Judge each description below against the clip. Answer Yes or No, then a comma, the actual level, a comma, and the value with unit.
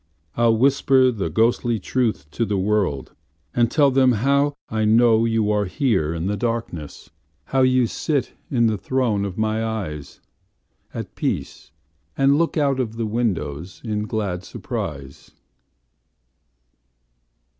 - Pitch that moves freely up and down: No, average, 4.1 semitones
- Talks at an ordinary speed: No, slow, 115 wpm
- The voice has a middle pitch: No, low, 115 Hz